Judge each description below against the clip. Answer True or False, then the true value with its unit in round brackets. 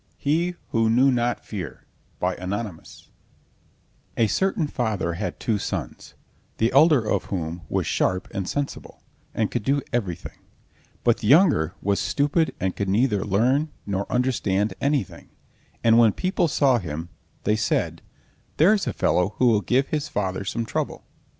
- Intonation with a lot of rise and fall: True (6.2 semitones)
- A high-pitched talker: False (115 Hz)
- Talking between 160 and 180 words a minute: False (150 wpm)